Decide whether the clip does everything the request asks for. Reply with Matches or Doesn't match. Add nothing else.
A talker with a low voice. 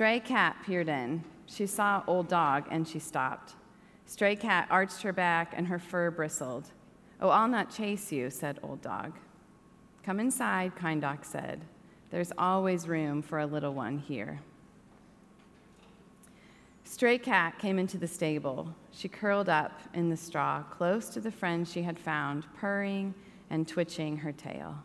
Doesn't match